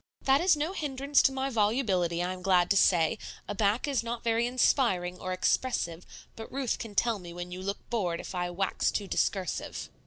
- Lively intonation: Yes, wide, 6.0 semitones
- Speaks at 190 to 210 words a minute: Yes, fast, 205 wpm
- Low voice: No, high, 205 Hz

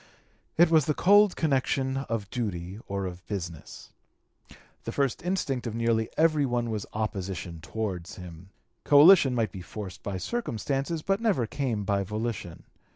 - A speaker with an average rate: Yes, average, 150 wpm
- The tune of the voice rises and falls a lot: Yes, wide, 6.6 semitones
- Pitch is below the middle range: Yes, low, 115 Hz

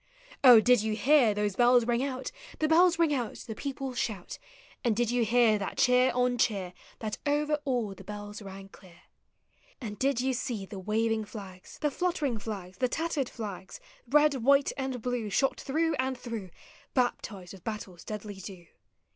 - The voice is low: No, high, 235 Hz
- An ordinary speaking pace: Yes, average, 175 wpm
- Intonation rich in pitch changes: No, average, 4.3 semitones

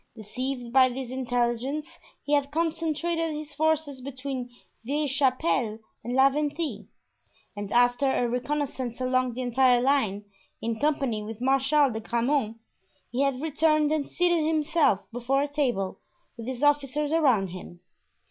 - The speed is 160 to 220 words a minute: No, average, 140 wpm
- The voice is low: No, very high, 265 Hz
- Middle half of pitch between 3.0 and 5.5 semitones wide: Yes, average, 3.5 semitones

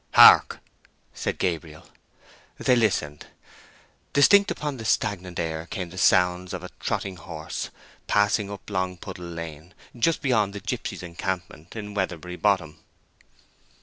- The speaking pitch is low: Yes, very low, 90 Hz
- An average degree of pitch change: Yes, average, 3.5 semitones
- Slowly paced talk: Yes, slow, 120 wpm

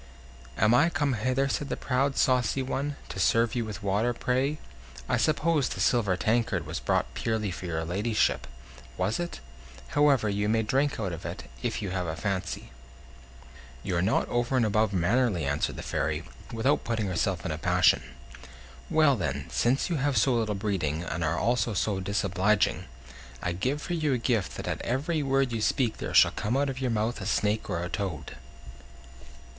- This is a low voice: Yes, low, 110 Hz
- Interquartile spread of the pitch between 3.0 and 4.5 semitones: No, wide, 5.6 semitones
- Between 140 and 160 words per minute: No, average, 185 wpm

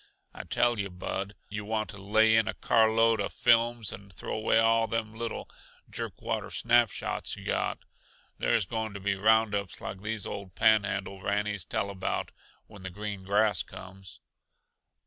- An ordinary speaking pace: Yes, average, 170 wpm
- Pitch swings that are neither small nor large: No, narrow, 2.2 semitones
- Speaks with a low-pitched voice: Yes, low, 105 Hz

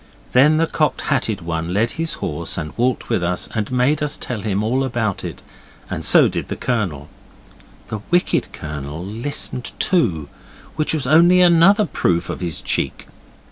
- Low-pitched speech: Yes, low, 120 Hz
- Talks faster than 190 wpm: No, average, 170 wpm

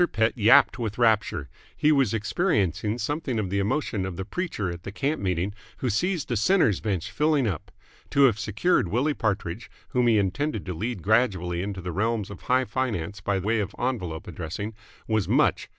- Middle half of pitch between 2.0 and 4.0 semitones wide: No, average, 4.8 semitones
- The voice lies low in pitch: Yes, low, 110 Hz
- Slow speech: No, average, 185 wpm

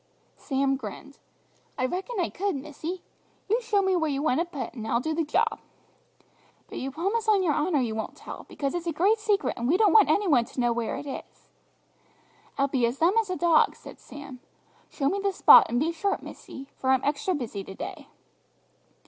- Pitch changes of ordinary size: No, wide, 6.1 semitones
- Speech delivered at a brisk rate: Yes, fast, 215 wpm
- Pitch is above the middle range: Yes, very high, 305 Hz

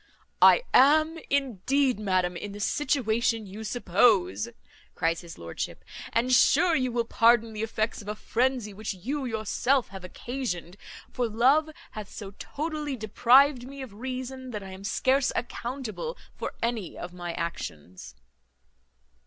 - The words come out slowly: No, average, 145 wpm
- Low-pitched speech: No, high, 230 Hz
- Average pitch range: Yes, average, 4.9 semitones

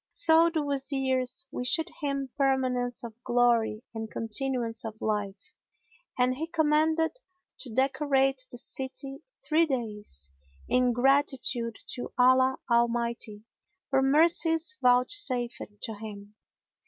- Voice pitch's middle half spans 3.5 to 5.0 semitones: No, average, 3.1 semitones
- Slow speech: Yes, slow, 110 wpm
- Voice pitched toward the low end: No, very high, 255 Hz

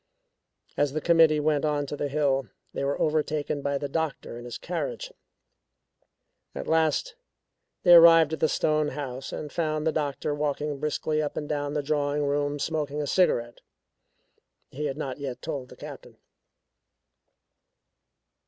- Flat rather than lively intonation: Yes, narrow, 1.6 semitones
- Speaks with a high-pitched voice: No, medium, 150 Hz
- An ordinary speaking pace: Yes, average, 155 wpm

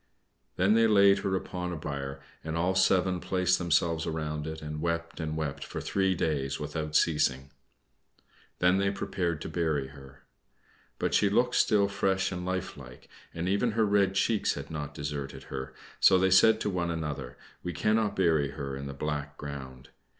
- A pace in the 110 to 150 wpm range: No, average, 180 wpm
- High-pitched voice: No, very low, 85 Hz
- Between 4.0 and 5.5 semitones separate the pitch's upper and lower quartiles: Yes, average, 4.4 semitones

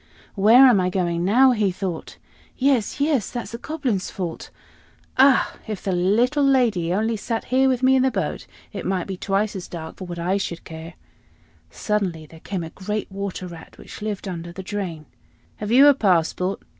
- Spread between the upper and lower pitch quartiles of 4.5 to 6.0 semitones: Yes, average, 5.3 semitones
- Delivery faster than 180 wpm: Yes, average, 190 wpm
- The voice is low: No, high, 200 Hz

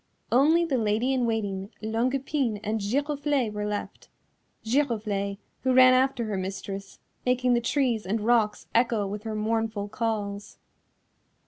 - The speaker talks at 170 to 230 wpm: No, average, 140 wpm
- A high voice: Yes, high, 225 Hz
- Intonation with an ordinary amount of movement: Yes, average, 3.5 semitones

